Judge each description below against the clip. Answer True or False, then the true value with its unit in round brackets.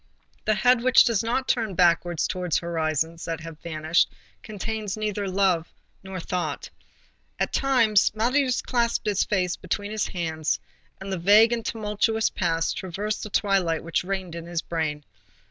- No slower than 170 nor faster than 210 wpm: False (155 wpm)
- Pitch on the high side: True (195 Hz)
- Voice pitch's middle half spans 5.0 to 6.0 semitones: False (4.3 semitones)